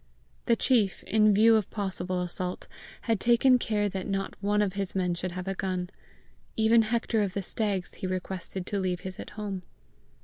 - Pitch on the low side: No, high, 195 Hz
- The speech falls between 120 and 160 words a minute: No, average, 190 wpm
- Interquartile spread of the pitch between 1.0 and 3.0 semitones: Yes, average, 2.7 semitones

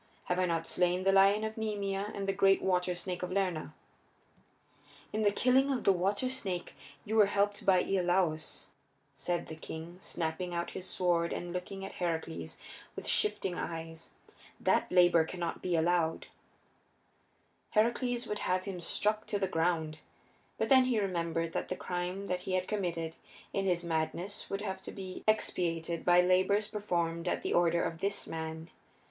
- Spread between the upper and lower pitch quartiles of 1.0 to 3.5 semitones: Yes, average, 2.8 semitones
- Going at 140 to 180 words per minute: Yes, average, 170 wpm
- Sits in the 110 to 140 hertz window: No, medium, 180 Hz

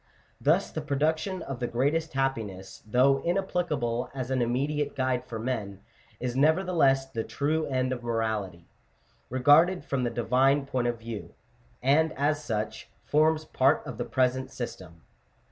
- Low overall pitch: Yes, low, 130 Hz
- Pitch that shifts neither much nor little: Yes, average, 3.7 semitones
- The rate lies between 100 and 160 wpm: Yes, average, 155 wpm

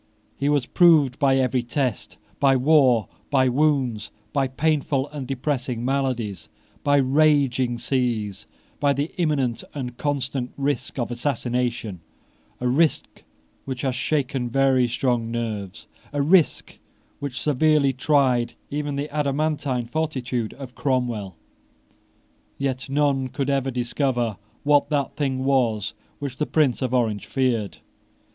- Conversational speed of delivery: No, slow, 125 wpm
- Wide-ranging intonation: No, average, 2.7 semitones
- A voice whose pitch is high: No, low, 130 Hz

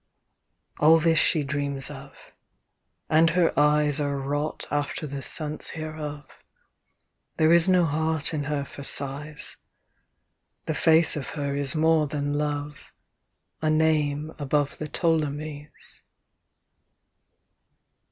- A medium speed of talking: No, slow, 120 wpm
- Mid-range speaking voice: Yes, medium, 150 Hz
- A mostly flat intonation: Yes, narrow, 1.6 semitones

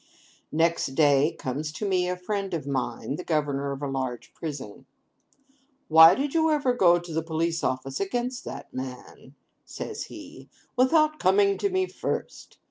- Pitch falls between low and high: Yes, medium, 165 Hz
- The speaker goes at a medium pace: Yes, average, 160 wpm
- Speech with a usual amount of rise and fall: No, wide, 6.3 semitones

